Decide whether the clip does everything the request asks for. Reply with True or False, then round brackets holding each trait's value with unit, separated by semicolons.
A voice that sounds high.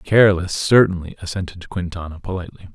False (90 Hz)